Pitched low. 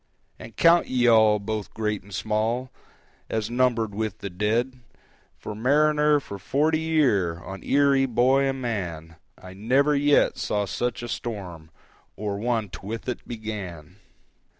Yes: low, 110 Hz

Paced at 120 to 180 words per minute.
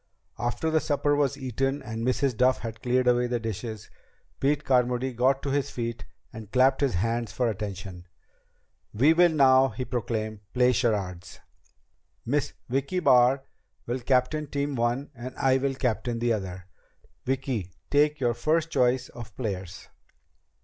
Yes: average, 150 wpm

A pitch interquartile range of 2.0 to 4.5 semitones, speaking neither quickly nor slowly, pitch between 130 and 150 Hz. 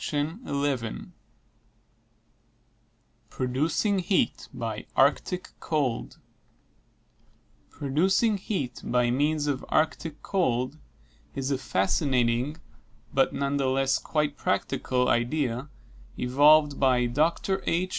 No: average, 3.8 semitones; slow, 85 wpm; medium, 140 Hz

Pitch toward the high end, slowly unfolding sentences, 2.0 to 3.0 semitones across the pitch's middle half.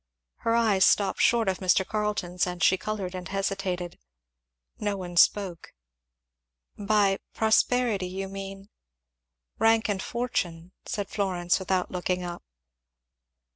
Yes: high, 195 Hz; slow, 125 wpm; average, 2.7 semitones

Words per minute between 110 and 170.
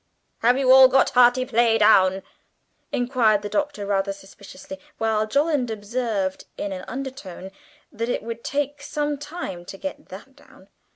Yes: average, 155 wpm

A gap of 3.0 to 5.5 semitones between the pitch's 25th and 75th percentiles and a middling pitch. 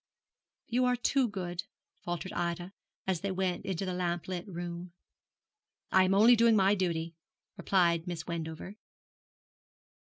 No: narrow, 2.4 semitones; medium, 180 Hz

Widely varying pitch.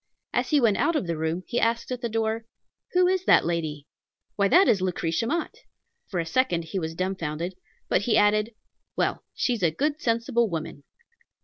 Yes: wide, 6.1 semitones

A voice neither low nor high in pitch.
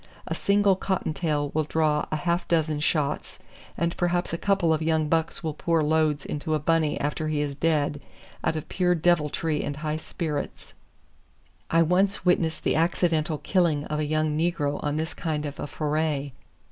Yes: medium, 155 Hz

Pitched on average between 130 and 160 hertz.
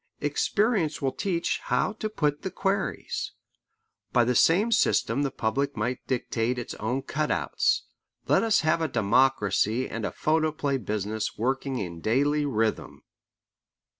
Yes: low, 135 Hz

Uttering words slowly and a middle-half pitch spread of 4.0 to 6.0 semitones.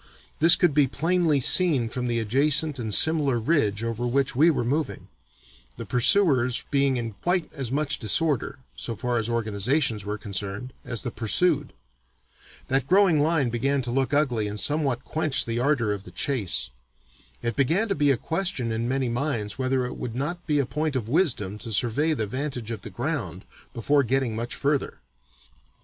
No: average, 180 wpm; average, 4.5 semitones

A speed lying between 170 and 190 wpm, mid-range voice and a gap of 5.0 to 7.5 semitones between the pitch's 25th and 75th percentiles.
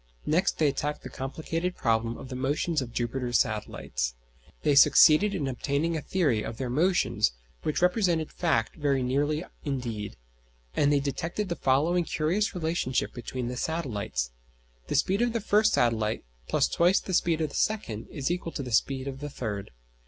Yes: average, 175 wpm; medium, 145 Hz; wide, 5.5 semitones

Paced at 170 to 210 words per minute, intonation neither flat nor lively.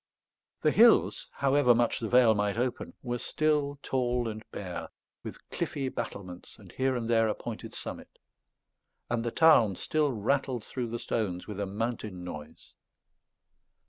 No: average, 150 wpm; average, 4.0 semitones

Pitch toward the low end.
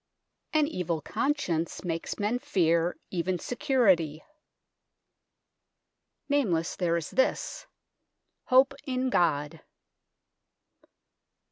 No: medium, 180 Hz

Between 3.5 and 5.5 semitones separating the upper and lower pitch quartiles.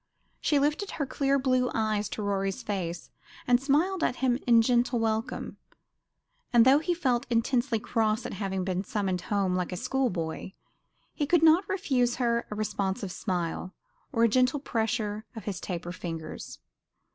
Yes: average, 5.1 semitones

